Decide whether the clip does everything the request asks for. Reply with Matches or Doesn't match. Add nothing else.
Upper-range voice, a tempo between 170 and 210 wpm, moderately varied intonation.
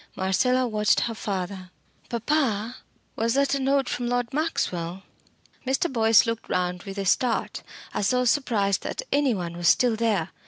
Doesn't match